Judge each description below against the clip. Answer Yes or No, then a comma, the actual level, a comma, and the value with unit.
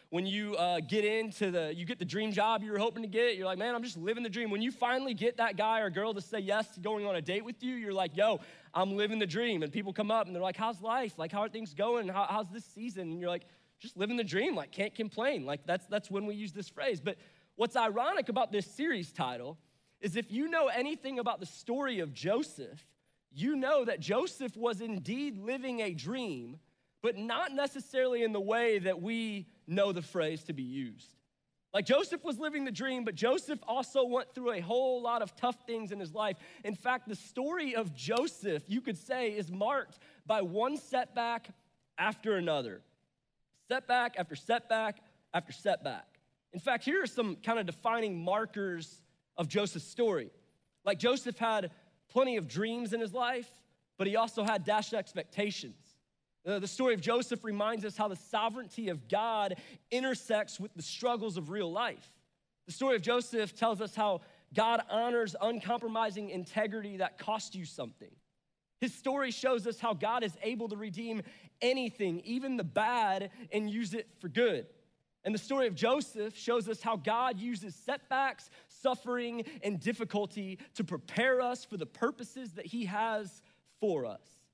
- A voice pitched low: No, high, 220 Hz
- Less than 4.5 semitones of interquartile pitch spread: Yes, average, 3.4 semitones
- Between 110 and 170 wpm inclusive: No, average, 190 wpm